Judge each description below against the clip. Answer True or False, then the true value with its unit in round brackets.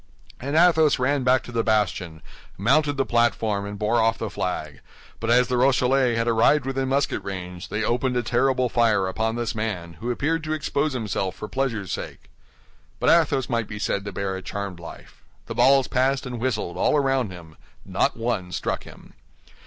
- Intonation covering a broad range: False (4.7 semitones)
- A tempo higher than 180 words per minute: True (190 wpm)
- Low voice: True (120 Hz)